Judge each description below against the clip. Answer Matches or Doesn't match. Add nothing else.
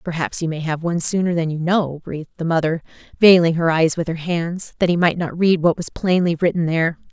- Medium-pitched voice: Matches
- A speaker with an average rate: Doesn't match